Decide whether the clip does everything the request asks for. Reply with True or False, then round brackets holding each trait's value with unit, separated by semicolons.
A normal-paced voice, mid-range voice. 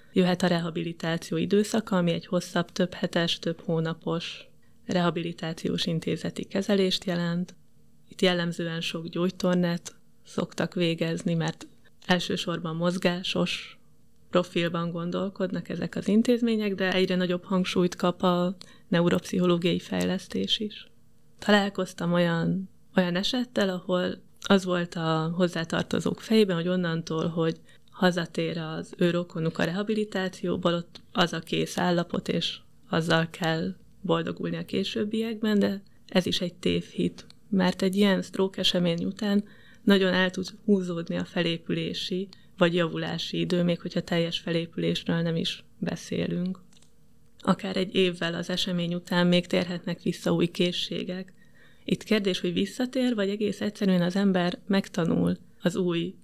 True (125 wpm; 180 Hz)